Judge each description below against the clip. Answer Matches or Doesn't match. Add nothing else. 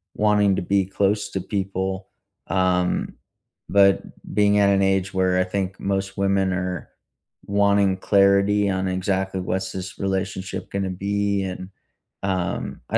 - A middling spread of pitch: Doesn't match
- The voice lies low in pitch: Matches